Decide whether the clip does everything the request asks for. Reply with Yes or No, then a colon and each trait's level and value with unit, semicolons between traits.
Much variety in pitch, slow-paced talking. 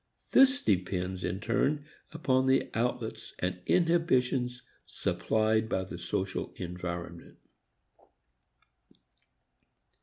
Yes: wide, 6.4 semitones; slow, 85 wpm